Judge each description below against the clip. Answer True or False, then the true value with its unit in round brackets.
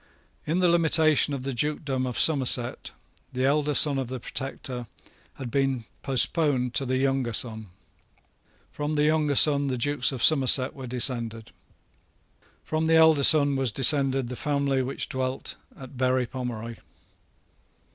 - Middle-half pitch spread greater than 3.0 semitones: False (2.6 semitones)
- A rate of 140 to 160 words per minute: True (145 wpm)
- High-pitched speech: False (135 Hz)